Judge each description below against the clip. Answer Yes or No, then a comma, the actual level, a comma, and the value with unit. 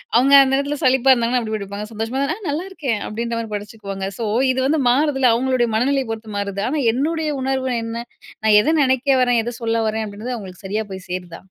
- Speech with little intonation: No, average, 3.7 semitones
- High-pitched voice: Yes, high, 240 Hz